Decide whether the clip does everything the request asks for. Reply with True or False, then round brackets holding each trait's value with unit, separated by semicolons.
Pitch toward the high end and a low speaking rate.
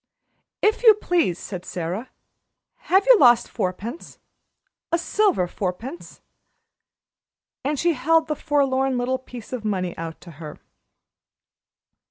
True (255 Hz; 120 wpm)